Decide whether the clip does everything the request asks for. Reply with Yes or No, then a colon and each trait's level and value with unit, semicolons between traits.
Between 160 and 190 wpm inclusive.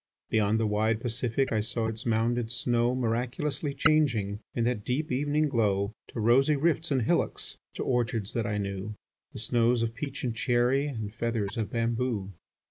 Yes: average, 170 wpm